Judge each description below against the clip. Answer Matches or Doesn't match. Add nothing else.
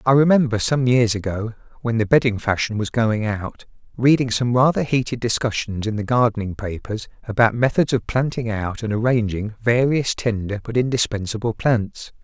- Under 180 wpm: Matches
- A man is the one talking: Matches